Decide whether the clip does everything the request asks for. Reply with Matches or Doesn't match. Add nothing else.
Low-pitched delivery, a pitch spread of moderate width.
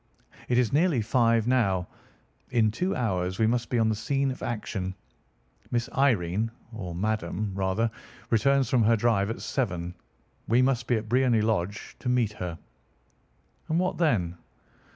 Matches